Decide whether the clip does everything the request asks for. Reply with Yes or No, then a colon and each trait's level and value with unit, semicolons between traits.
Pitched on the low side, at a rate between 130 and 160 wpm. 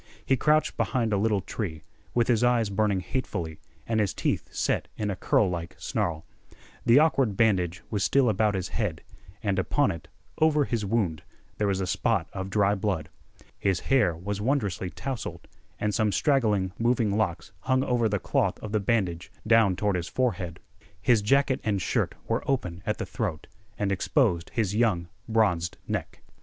No: low, 105 Hz; average, 175 wpm